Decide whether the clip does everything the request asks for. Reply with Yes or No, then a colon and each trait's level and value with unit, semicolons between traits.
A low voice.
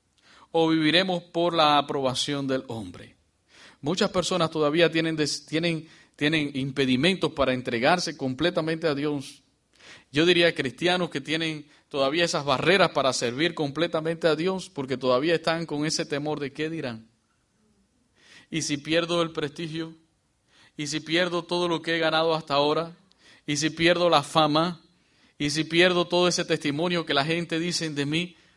No: medium, 160 Hz